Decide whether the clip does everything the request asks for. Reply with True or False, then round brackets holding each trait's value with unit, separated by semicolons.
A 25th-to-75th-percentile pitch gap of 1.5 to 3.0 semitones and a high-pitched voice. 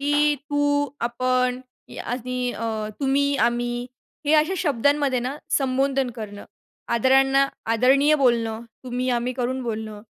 True (2.7 semitones; 255 Hz)